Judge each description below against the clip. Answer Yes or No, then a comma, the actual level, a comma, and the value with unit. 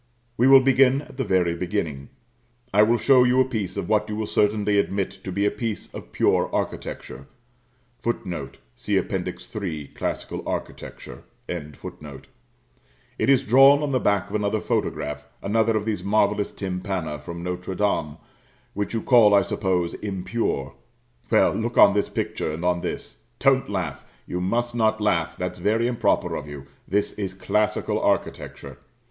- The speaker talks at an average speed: Yes, average, 160 wpm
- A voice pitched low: Yes, low, 100 Hz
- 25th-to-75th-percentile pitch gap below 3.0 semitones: No, average, 4.2 semitones